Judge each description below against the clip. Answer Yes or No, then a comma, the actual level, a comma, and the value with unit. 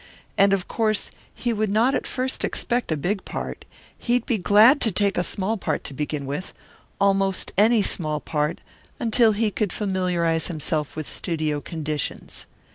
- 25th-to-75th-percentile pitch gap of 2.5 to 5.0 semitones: No, wide, 5.4 semitones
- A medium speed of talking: Yes, average, 170 wpm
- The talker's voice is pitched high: Yes, high, 195 Hz